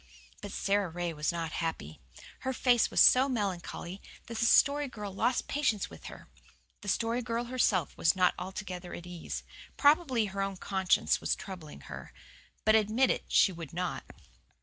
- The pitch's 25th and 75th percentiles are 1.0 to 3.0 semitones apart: No, average, 5.1 semitones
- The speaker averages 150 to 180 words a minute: Yes, average, 170 wpm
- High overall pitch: Yes, high, 200 Hz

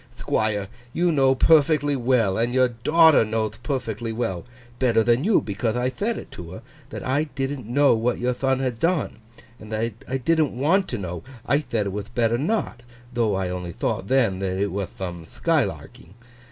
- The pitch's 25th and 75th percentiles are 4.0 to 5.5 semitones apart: Yes, average, 4.7 semitones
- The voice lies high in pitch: No, low, 120 Hz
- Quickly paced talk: No, average, 180 wpm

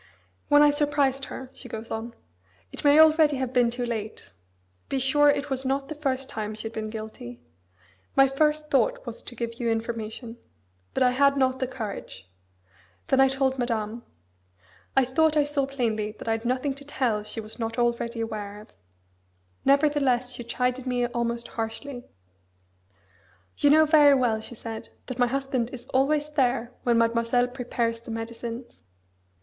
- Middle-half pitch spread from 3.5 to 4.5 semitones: No, average, 3.1 semitones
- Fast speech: No, average, 170 wpm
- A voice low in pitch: No, very high, 250 Hz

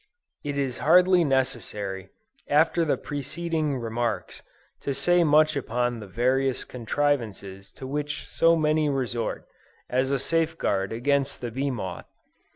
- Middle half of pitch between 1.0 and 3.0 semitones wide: No, average, 4.2 semitones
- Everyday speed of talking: No, slow, 130 wpm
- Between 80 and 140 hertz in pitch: Yes, low, 135 Hz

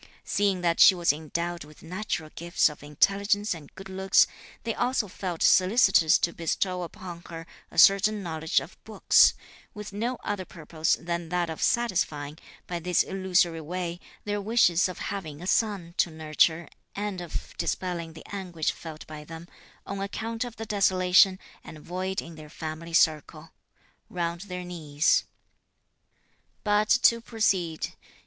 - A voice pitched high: No, medium, 180 Hz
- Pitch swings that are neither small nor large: Yes, average, 3.3 semitones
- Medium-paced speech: Yes, average, 150 wpm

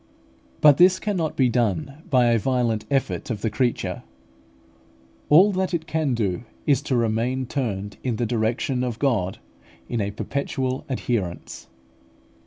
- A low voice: Yes, low, 125 Hz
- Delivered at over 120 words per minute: Yes, average, 145 wpm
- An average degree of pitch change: Yes, average, 3.9 semitones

